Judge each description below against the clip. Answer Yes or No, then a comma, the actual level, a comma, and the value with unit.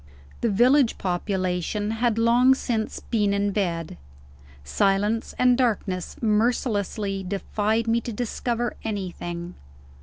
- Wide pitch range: No, average, 3.2 semitones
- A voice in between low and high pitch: No, high, 210 Hz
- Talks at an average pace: No, slow, 110 wpm